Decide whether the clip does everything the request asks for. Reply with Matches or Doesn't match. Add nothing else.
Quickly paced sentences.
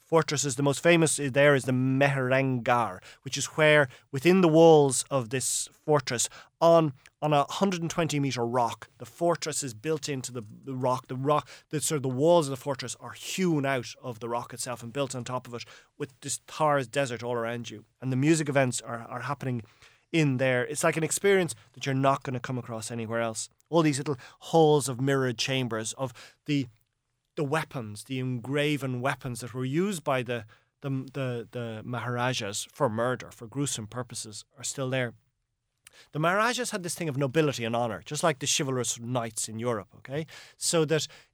Doesn't match